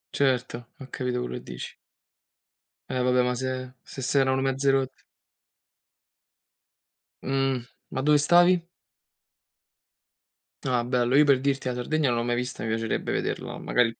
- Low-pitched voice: Yes, low, 130 Hz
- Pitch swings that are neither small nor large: No, narrow, 1.7 semitones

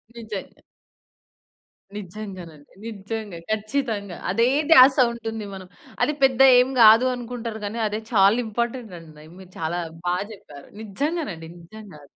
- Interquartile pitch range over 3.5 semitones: Yes, average, 4.0 semitones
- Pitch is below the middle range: No, high, 215 Hz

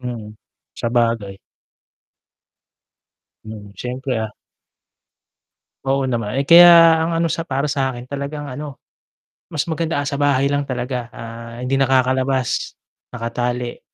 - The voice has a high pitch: No, low, 130 Hz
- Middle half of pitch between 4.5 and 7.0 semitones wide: No, average, 3.1 semitones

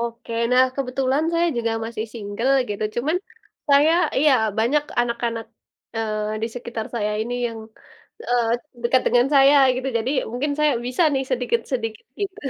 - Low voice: No, high, 245 Hz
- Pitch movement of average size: Yes, average, 3.0 semitones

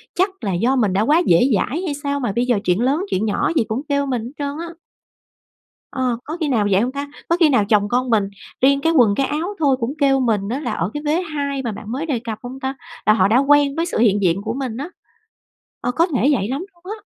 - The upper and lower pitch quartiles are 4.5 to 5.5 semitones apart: Yes, average, 4.8 semitones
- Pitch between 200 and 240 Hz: No, very high, 260 Hz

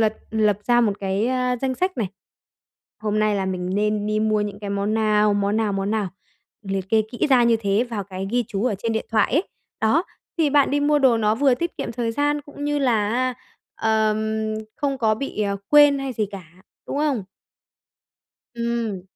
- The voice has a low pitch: No, high, 220 Hz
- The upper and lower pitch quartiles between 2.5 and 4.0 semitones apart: Yes, average, 3.6 semitones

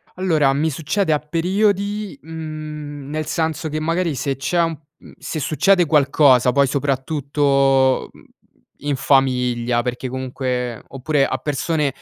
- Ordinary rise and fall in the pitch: Yes, average, 3.2 semitones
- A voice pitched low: No, medium, 145 Hz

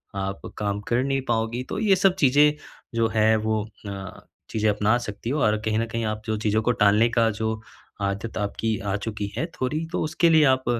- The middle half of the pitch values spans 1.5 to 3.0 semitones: No, average, 3.6 semitones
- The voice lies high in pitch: No, low, 110 Hz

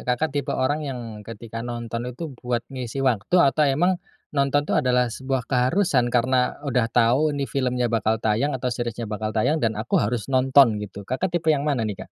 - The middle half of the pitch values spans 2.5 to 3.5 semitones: Yes, average, 2.9 semitones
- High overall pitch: No, low, 125 Hz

